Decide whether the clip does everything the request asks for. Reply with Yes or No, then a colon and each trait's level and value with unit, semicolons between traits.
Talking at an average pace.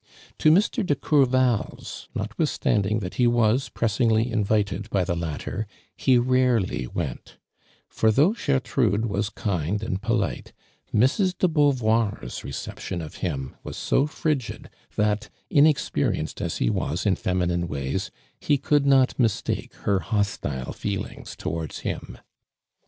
No: slow, 130 wpm